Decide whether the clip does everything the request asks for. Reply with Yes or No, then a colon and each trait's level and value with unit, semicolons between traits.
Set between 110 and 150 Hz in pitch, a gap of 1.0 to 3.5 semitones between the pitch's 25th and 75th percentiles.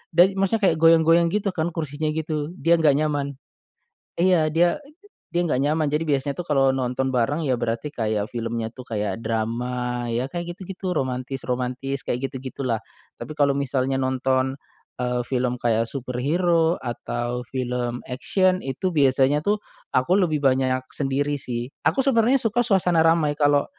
No: medium, 140 Hz; average, 4.8 semitones